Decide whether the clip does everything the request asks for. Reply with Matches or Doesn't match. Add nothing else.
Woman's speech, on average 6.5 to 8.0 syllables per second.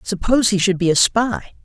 Doesn't match